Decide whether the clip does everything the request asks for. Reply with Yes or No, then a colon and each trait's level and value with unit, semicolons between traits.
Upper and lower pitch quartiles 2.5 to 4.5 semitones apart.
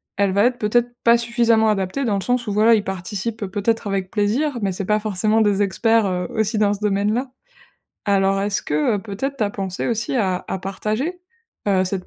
Yes: average, 2.8 semitones